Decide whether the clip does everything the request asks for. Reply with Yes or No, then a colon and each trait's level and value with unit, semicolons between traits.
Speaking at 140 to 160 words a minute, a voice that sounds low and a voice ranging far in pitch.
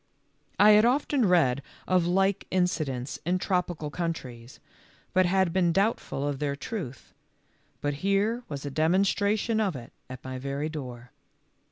No: average, 145 wpm; medium, 170 Hz; wide, 5.9 semitones